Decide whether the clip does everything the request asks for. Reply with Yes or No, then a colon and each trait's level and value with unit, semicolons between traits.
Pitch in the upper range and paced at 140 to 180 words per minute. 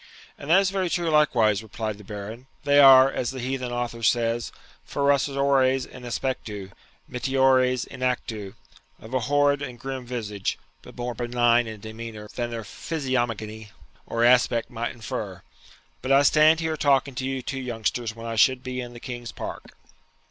No: low, 125 Hz; average, 170 wpm